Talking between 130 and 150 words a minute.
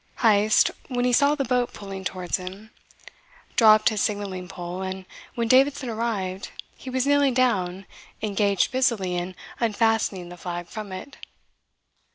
Yes: average, 145 wpm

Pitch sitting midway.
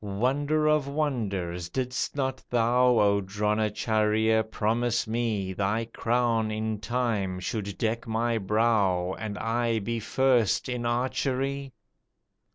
No: low, 115 Hz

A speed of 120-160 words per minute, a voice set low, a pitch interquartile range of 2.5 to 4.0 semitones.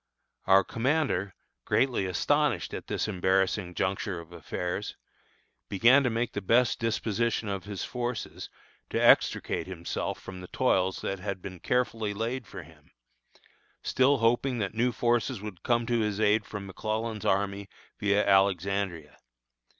Yes: average, 140 wpm; low, 105 Hz; average, 3.7 semitones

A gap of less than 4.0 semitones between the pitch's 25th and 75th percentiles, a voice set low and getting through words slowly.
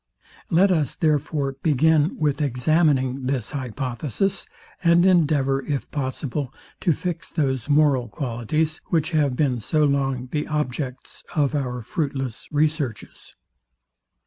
No: average, 3.0 semitones; medium, 145 Hz; slow, 120 wpm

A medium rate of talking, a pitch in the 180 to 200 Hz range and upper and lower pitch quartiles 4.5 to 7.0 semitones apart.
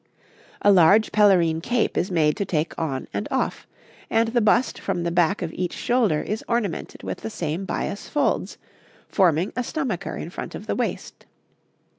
Yes: average, 175 wpm; high, 190 Hz; average, 5.2 semitones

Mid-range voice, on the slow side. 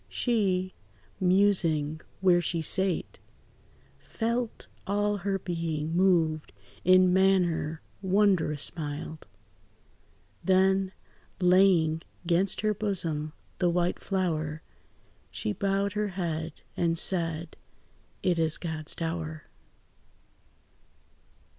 Yes: medium, 180 Hz; slow, 90 wpm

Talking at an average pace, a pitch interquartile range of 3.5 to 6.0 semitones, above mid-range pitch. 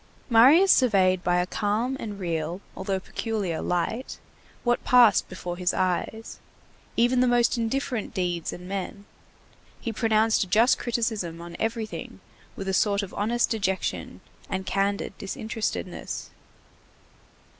No: slow, 130 wpm; average, 3.9 semitones; high, 205 Hz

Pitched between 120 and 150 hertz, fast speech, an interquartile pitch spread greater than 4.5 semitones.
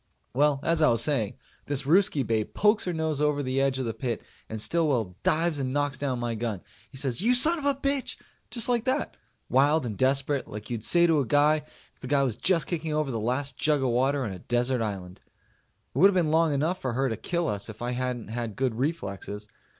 Yes: low, 135 Hz; fast, 235 wpm; average, 5.0 semitones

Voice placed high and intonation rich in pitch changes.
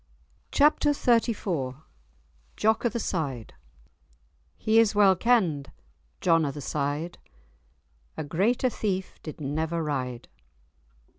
No: medium, 170 Hz; wide, 7.2 semitones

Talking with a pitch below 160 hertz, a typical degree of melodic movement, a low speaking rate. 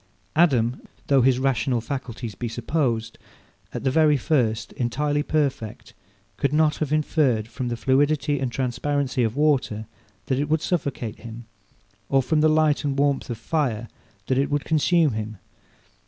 No: low, 135 Hz; average, 3.9 semitones; average, 155 wpm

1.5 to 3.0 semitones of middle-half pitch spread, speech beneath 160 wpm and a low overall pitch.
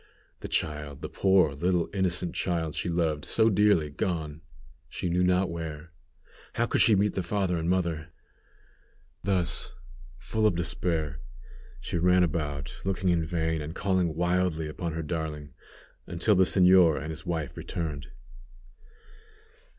Yes: narrow, 2.6 semitones; average, 145 wpm; very low, 85 Hz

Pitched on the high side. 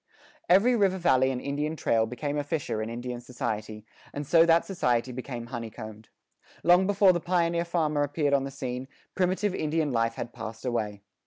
No: medium, 140 Hz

